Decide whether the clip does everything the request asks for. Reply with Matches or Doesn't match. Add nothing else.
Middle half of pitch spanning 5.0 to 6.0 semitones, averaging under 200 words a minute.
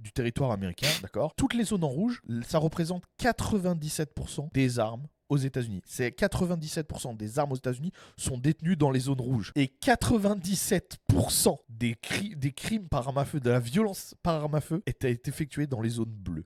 Matches